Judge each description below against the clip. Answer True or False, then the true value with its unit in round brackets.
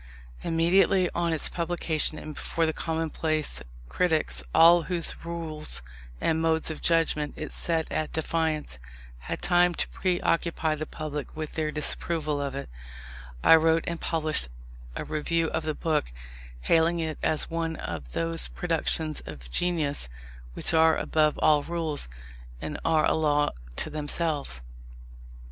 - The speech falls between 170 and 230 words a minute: False (145 wpm)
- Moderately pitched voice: True (160 Hz)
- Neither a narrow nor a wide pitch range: False (1.6 semitones)